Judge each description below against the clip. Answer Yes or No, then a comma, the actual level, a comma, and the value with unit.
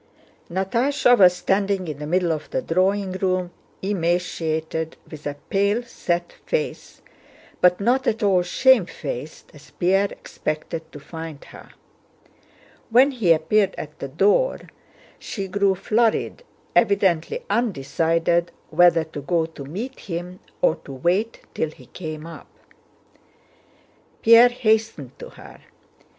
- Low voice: No, medium, 180 Hz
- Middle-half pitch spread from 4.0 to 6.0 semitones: Yes, average, 4.3 semitones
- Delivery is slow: Yes, slow, 125 wpm